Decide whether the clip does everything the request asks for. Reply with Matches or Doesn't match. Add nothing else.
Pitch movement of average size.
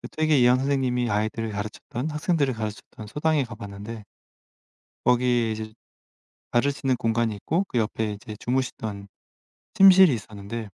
Matches